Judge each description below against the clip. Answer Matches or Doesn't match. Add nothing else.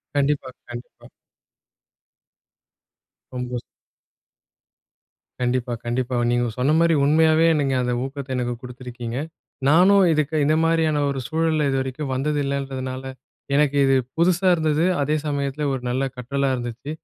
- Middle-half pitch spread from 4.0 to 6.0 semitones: Doesn't match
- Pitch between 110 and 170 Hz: Matches